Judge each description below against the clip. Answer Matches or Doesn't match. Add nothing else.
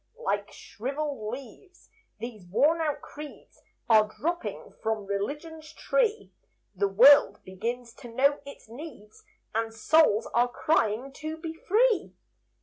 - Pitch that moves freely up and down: Matches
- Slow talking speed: Matches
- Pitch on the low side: Doesn't match